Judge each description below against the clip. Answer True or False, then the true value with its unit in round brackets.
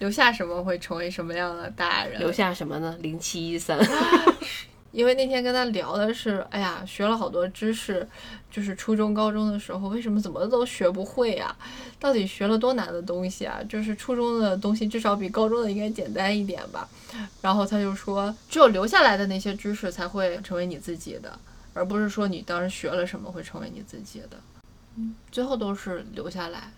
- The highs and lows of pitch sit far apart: False (3.6 semitones)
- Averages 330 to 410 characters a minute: False (305 characters per minute)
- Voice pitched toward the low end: False (200 Hz)